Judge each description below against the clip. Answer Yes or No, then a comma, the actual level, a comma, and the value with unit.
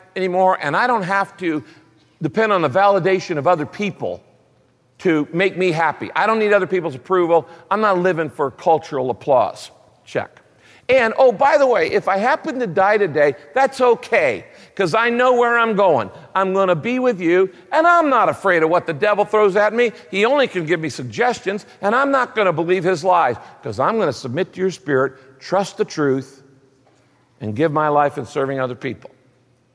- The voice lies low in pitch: No, medium, 185 Hz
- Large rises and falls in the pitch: Yes, wide, 6.2 semitones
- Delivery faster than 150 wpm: Yes, average, 200 wpm